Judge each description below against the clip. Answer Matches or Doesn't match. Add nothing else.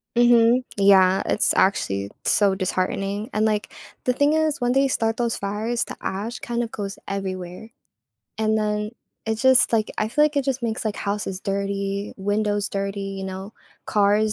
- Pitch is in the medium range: Doesn't match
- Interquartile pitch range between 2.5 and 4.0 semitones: Matches